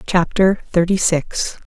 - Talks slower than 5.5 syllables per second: Yes, 3.7 syllables/s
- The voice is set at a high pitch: No, medium, 180 Hz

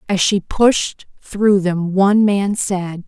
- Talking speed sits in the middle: Yes, average, 155 wpm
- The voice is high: Yes, high, 195 Hz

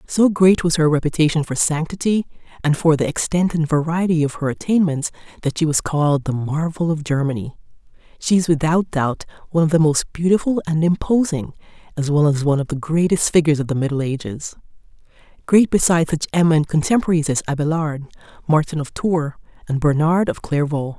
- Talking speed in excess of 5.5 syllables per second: Yes, 5.9 syllables/s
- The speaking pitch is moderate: Yes, medium, 160 Hz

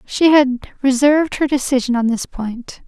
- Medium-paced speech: Yes, average, 165 wpm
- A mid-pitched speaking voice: No, very high, 265 Hz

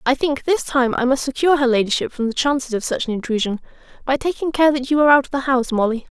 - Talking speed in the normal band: No, fast, 265 wpm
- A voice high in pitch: Yes, very high, 265 Hz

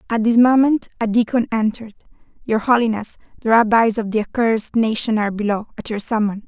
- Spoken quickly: No, average, 175 wpm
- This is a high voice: Yes, high, 225 Hz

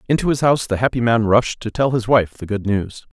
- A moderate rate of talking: No, fast, 265 wpm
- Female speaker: No, male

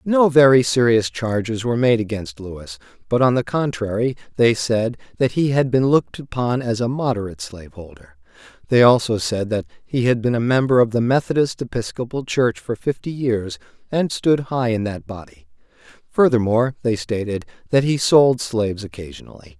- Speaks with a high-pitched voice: No, low, 115 Hz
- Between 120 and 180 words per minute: Yes, average, 170 wpm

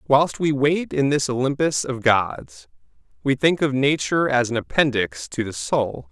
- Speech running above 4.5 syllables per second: No, 4.4 syllables/s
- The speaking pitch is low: Yes, low, 130 Hz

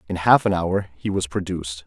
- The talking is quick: Yes, fast, 225 wpm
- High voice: No, very low, 90 Hz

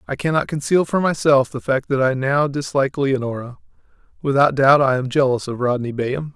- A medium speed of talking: Yes, average, 190 wpm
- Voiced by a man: Yes, male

